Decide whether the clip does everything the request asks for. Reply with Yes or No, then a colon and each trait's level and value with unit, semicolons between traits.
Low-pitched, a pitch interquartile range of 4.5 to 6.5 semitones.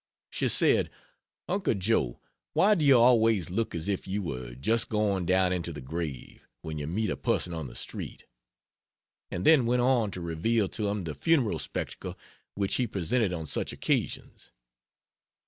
Yes: low, 100 Hz; wide, 5.6 semitones